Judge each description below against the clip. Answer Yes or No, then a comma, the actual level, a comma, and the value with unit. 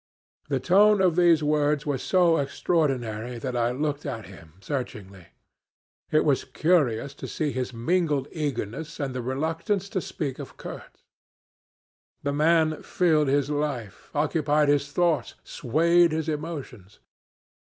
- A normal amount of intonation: Yes, average, 4.0 semitones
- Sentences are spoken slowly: Yes, slow, 130 wpm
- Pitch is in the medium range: Yes, medium, 145 Hz